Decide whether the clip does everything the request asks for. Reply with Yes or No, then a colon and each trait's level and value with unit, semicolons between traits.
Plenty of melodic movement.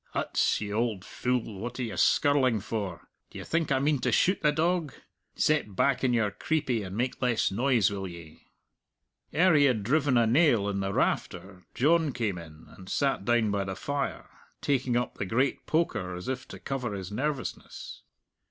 Yes: wide, 5.8 semitones